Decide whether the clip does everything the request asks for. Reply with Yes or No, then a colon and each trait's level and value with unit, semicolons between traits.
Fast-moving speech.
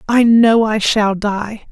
No: average, 175 wpm